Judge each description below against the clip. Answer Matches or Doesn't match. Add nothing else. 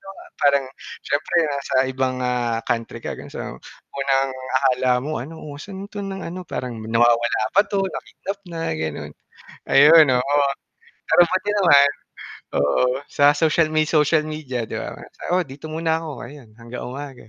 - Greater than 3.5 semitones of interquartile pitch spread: Matches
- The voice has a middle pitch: Matches